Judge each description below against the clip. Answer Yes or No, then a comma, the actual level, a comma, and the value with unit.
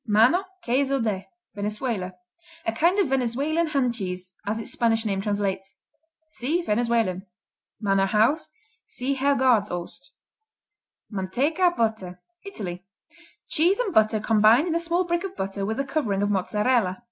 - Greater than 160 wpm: No, slow, 135 wpm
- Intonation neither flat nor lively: No, wide, 5.8 semitones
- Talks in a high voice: Yes, high, 225 Hz